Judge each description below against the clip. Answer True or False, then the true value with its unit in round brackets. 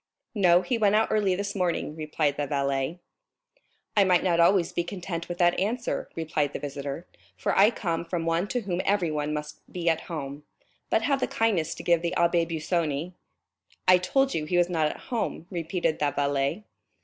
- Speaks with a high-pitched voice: False (170 Hz)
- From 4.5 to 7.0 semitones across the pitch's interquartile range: False (3.8 semitones)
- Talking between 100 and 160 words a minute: False (190 wpm)